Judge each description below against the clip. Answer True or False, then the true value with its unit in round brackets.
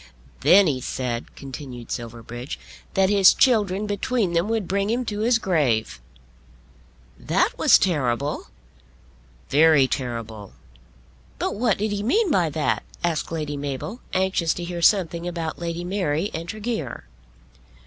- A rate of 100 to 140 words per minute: True (135 wpm)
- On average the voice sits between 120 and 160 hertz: False (170 Hz)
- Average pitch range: False (6.5 semitones)